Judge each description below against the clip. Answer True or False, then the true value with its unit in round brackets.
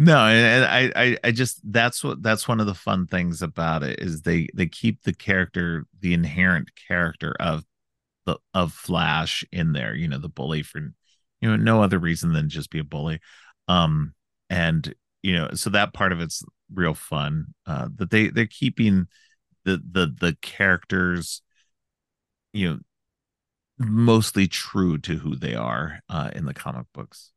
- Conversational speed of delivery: True (175 wpm)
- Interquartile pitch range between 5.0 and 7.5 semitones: True (5.4 semitones)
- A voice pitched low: True (95 Hz)